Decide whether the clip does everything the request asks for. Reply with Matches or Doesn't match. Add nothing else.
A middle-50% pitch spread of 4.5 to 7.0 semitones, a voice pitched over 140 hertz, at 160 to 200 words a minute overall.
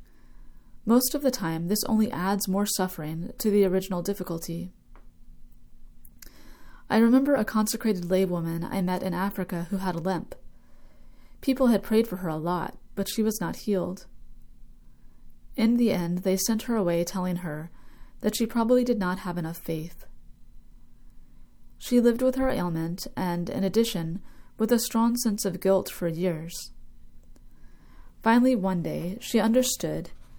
Doesn't match